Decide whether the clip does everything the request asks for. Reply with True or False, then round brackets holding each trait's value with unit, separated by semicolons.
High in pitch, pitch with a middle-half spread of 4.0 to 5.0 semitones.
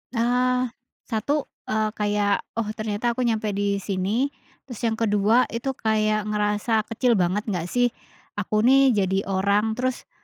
False (215 Hz; 2.7 semitones)